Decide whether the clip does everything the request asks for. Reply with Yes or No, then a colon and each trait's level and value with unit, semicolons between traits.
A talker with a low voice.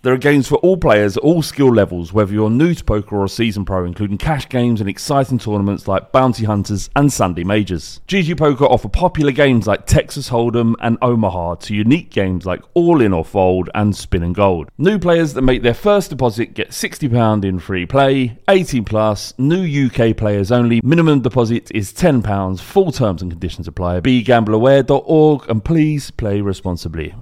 Yes: low, 115 Hz